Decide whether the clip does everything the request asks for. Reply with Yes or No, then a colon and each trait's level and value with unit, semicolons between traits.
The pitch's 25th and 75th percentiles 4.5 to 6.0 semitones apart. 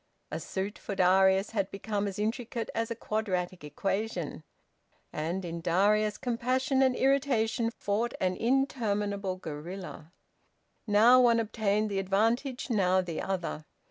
No: average, 3.6 semitones